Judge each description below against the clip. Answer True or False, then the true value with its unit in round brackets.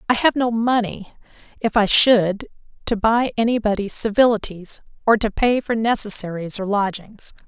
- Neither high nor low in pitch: False (215 Hz)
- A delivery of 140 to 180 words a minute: True (150 wpm)